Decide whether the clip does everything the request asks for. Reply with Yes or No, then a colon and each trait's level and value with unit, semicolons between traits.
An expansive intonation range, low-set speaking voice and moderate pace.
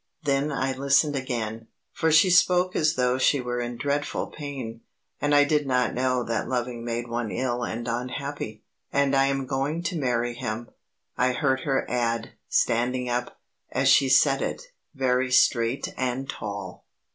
No: average, 2.7 semitones; low, 130 Hz; average, 165 wpm